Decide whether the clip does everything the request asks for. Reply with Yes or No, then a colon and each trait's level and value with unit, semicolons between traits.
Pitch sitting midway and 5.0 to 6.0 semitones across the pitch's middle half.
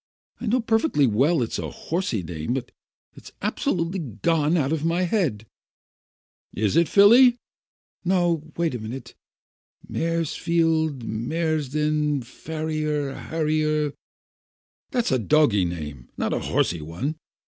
Yes: medium, 155 Hz; wide, 5.4 semitones